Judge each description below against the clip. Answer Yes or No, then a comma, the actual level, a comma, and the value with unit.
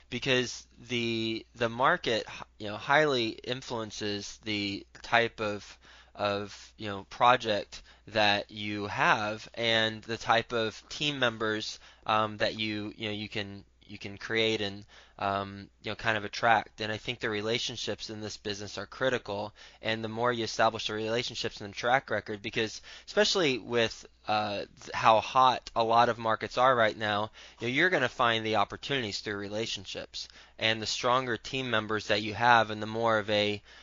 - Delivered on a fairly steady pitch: Yes, narrow, 2.0 semitones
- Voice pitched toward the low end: Yes, low, 110 Hz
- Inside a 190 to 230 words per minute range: No, average, 170 wpm